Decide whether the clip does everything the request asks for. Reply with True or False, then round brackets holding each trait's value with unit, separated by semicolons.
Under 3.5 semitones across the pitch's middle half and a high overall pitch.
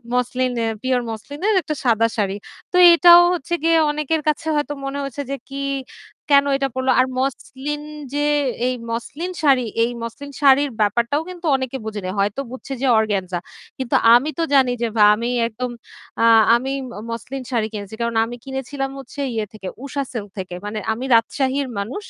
False (3.8 semitones; 260 Hz)